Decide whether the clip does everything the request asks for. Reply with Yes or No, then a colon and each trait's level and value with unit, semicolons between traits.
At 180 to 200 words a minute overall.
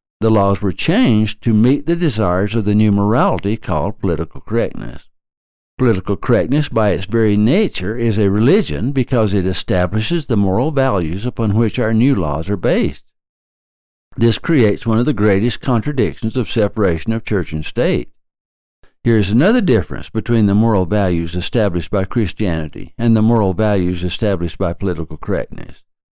No: average, 160 wpm